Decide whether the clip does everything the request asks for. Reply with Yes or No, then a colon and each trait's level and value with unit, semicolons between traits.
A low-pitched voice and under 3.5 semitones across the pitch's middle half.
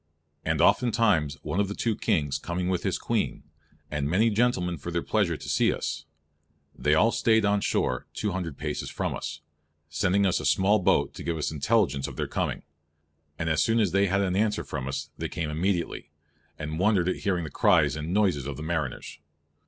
No: very low, 90 Hz; average, 4.9 semitones